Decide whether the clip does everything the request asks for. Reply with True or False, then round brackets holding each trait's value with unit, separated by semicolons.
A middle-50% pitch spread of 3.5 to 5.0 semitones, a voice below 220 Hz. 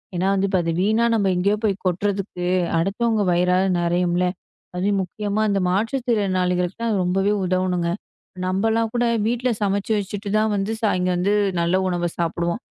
False (2.9 semitones; 195 Hz)